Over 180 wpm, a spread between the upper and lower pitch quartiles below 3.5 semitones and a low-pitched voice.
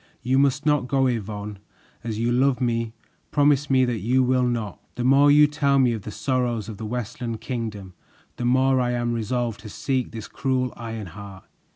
Yes: average, 190 wpm; average, 2.9 semitones; low, 120 Hz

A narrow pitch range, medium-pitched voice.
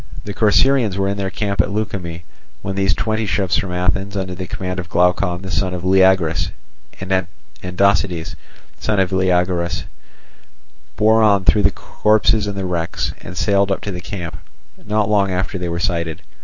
No: narrow, 2.1 semitones; very low, 95 Hz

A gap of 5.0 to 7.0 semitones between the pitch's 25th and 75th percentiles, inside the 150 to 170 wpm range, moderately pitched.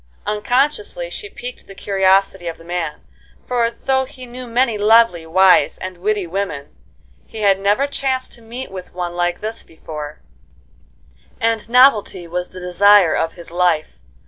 No: average, 5.3 semitones; average, 155 wpm; high, 200 Hz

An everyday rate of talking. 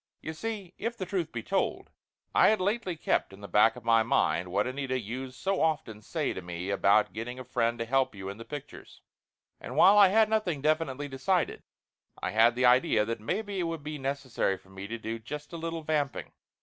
No: fast, 220 wpm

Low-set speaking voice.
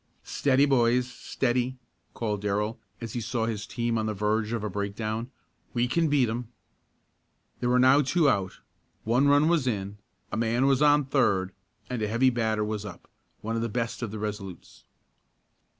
Yes: low, 115 Hz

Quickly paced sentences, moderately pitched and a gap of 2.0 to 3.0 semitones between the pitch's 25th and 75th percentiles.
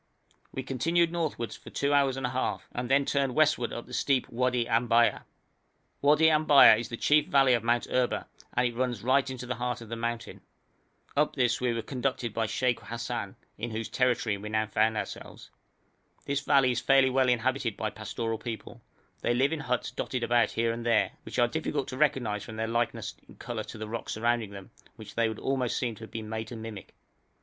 No: fast, 210 wpm; low, 120 Hz; average, 2.7 semitones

